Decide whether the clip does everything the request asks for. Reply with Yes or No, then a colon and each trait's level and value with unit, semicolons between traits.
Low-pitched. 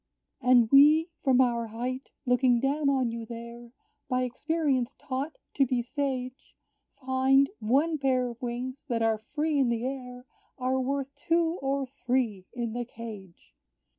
No: very high, 255 Hz